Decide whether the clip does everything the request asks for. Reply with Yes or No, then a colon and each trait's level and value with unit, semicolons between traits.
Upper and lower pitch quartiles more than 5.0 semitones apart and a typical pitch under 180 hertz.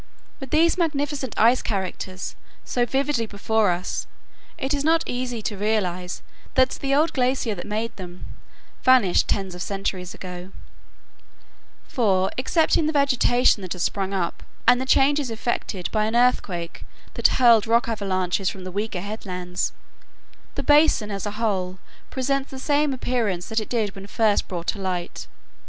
No: wide, 5.5 semitones; high, 220 Hz